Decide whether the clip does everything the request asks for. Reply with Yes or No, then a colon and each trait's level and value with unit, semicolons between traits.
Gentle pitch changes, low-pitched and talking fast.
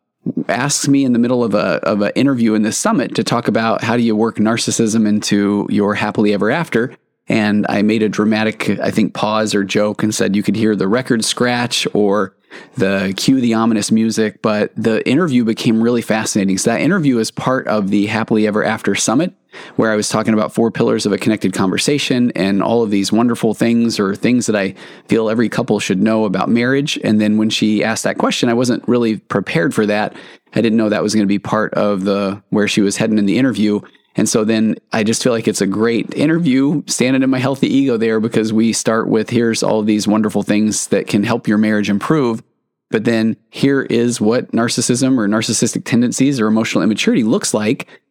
Yes: narrow, 2.0 semitones; low, 110 Hz; fast, 215 wpm